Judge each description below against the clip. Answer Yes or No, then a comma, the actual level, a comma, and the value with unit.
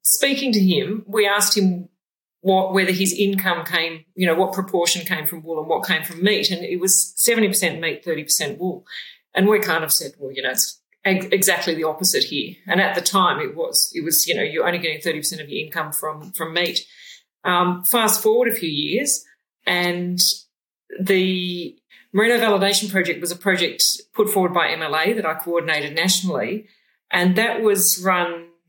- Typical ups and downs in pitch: Yes, average, 3.4 semitones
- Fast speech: No, average, 190 wpm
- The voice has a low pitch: No, medium, 185 Hz